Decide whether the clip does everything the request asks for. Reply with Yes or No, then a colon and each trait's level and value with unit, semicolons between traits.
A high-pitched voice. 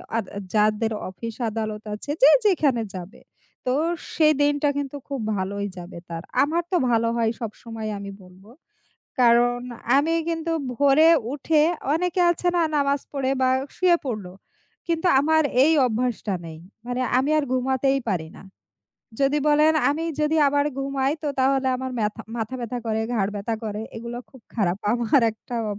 Yes: very high, 250 Hz